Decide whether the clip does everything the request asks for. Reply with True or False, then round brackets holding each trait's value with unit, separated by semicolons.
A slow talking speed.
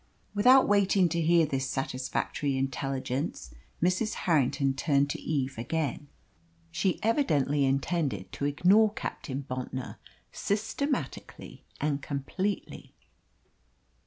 True (100 wpm)